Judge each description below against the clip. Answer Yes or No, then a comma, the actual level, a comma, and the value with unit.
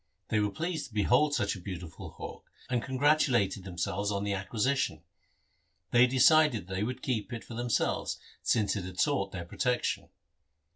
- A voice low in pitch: Yes, low, 110 Hz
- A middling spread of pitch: Yes, average, 4.7 semitones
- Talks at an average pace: Yes, average, 165 wpm